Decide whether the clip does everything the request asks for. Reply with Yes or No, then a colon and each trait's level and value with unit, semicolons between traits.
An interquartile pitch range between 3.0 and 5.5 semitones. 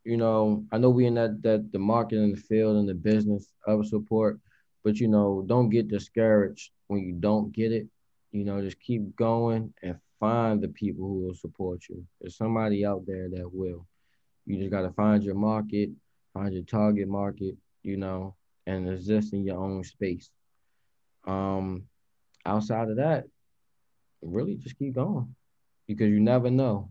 No: narrow, 2.6 semitones